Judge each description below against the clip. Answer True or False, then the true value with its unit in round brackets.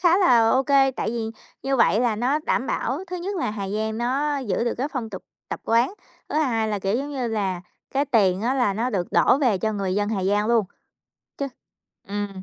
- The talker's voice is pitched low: False (235 Hz)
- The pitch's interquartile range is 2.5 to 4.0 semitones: False (4.6 semitones)